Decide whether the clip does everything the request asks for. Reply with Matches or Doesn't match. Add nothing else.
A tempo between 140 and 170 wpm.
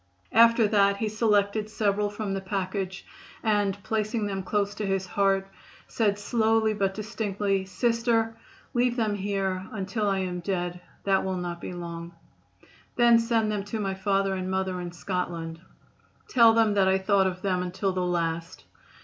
Matches